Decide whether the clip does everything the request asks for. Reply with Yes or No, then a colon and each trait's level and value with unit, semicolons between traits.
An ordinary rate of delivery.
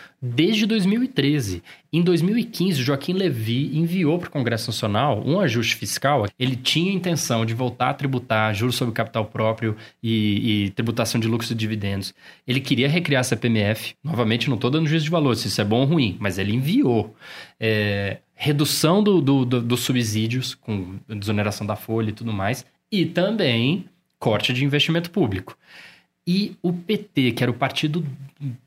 Yes: average, 170 wpm